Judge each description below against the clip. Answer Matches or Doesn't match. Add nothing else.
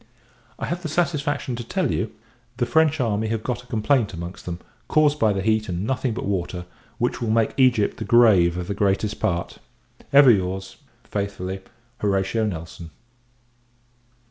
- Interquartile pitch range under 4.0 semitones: Doesn't match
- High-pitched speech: Doesn't match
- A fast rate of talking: Doesn't match